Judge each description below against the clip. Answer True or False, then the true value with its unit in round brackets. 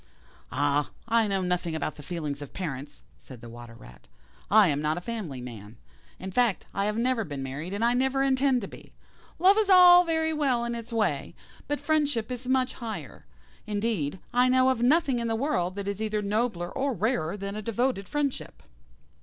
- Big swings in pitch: True (8.0 semitones)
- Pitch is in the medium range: False (215 Hz)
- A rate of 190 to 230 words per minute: True (195 wpm)